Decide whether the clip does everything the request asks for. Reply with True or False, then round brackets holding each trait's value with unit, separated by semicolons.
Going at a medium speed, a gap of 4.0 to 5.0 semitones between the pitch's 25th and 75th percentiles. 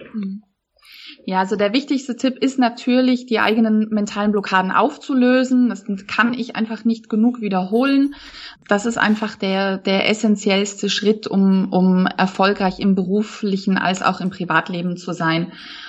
False (140 wpm; 3.3 semitones)